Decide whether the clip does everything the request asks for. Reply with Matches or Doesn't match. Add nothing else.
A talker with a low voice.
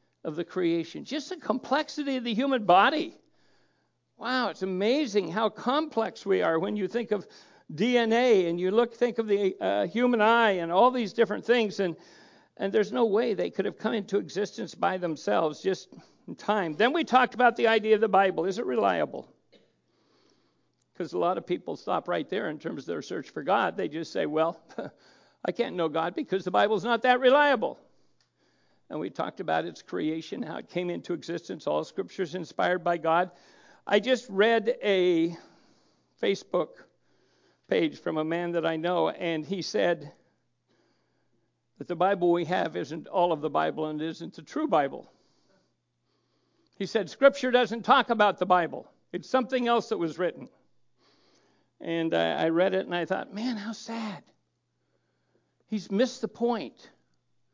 Doesn't match